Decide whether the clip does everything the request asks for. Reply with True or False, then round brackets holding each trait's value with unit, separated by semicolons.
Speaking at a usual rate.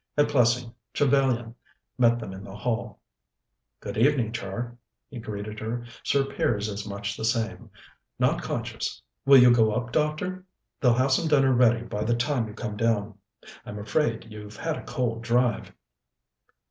True (160 wpm)